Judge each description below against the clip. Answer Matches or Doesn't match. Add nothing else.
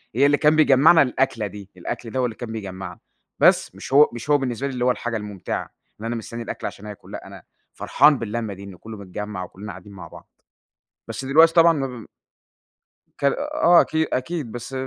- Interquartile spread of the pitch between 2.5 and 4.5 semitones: Doesn't match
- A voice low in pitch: Matches